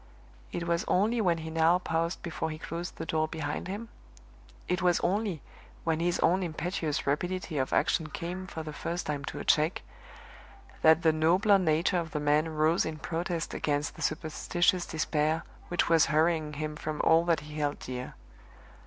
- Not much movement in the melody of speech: Yes, narrow, 2.2 semitones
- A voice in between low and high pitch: Yes, medium, 165 Hz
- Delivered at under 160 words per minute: No, average, 180 wpm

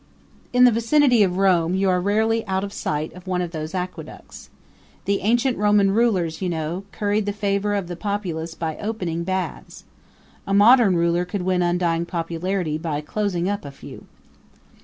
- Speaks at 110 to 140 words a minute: No, average, 175 wpm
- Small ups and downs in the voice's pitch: No, average, 3.2 semitones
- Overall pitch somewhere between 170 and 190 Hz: Yes, medium, 185 Hz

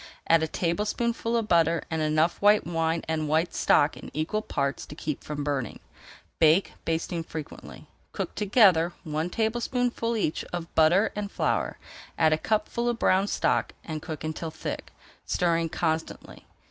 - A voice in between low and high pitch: Yes, medium, 165 Hz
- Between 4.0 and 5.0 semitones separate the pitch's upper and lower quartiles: Yes, average, 4.7 semitones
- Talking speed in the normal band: Yes, average, 155 wpm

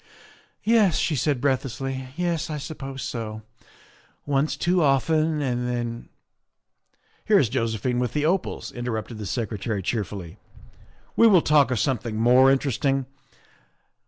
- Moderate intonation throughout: Yes, average, 4.4 semitones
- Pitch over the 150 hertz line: No, low, 130 Hz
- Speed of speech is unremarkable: Yes, average, 150 wpm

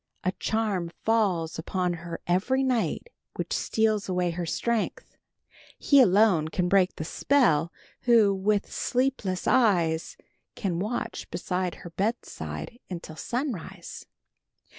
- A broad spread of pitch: No, average, 4.7 semitones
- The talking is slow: Yes, slow, 120 wpm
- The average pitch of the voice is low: No, high, 190 Hz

